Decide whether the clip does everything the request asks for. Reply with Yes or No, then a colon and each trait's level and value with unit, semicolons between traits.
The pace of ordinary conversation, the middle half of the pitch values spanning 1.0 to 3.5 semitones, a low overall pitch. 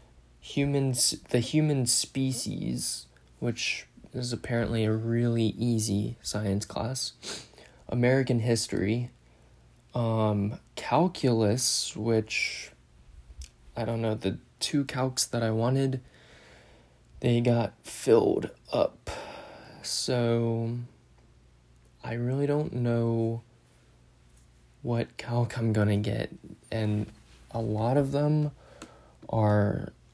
No: slow, 90 wpm; average, 3.2 semitones; low, 115 Hz